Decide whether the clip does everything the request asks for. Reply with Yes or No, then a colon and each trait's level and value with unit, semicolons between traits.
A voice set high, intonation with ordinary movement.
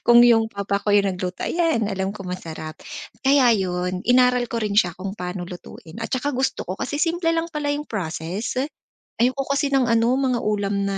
No: high, 225 Hz; wide, 5.8 semitones